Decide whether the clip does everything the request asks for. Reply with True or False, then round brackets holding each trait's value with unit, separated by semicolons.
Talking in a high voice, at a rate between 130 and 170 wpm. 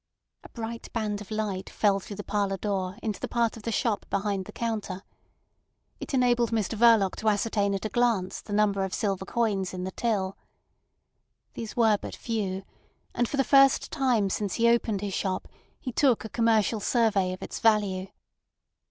False (210 Hz; 185 wpm)